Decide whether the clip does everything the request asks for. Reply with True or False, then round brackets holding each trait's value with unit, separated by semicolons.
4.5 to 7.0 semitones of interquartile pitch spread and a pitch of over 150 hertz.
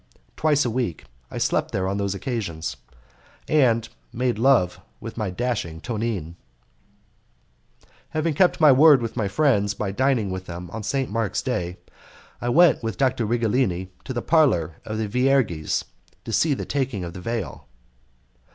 False (5.6 semitones; 115 Hz)